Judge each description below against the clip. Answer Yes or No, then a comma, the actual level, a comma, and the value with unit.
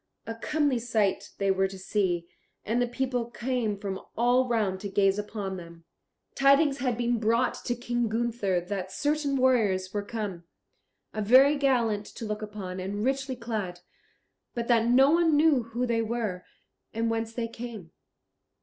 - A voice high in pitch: Yes, high, 230 Hz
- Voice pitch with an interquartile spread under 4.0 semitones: Yes, average, 3.6 semitones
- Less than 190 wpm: Yes, average, 160 wpm